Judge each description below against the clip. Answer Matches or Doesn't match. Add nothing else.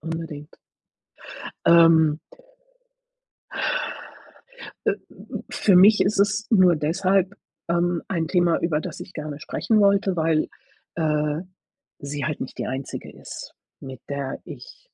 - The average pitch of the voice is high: Doesn't match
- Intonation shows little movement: Doesn't match